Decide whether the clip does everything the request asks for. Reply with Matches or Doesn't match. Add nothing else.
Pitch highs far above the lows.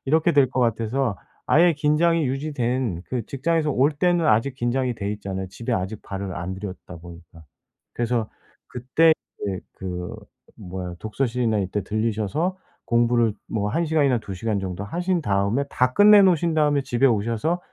Matches